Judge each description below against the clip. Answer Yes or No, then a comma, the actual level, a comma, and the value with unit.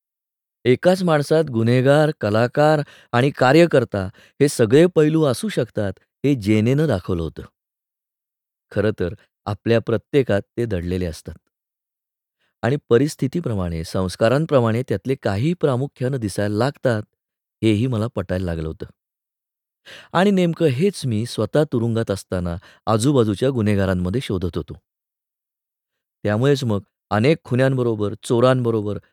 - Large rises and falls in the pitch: Yes, wide, 5.9 semitones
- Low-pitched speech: Yes, low, 115 Hz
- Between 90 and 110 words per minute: Yes, average, 105 wpm